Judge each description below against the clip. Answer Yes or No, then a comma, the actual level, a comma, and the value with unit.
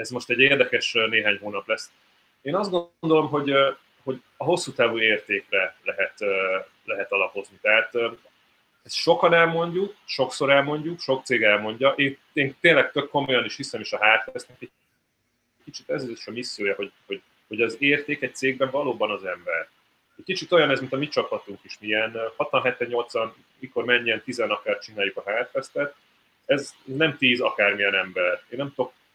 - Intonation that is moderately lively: No, wide, 6.3 semitones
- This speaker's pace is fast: Yes, fast, 165 wpm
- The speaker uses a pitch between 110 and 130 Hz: No, medium, 140 Hz